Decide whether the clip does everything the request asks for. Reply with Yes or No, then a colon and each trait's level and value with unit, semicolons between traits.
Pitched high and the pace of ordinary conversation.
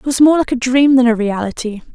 No: high, 245 Hz; fast, 275 wpm